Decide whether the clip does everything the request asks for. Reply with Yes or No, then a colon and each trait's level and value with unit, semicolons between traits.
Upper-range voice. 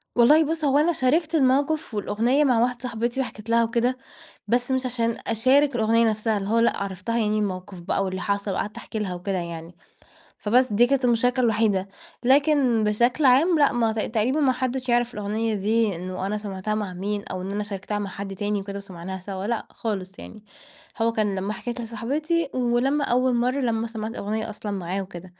Yes: high, 225 Hz